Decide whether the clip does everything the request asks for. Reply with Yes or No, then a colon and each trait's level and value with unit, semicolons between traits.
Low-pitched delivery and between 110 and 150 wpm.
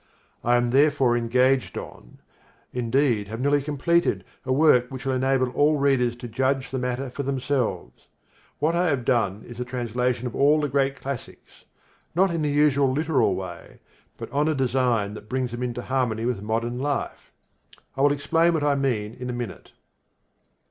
No: low, 130 Hz; average, 175 wpm